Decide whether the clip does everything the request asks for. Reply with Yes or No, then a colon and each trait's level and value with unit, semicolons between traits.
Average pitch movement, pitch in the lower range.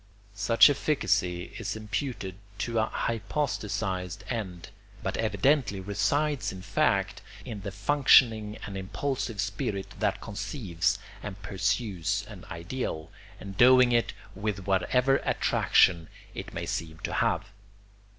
Yes: average, 3.6 semitones; low, 105 Hz